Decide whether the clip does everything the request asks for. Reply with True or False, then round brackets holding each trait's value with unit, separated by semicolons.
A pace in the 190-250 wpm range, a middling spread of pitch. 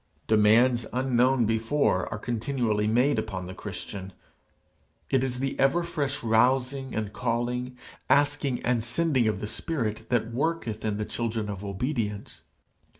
False (145 wpm; 3.5 semitones)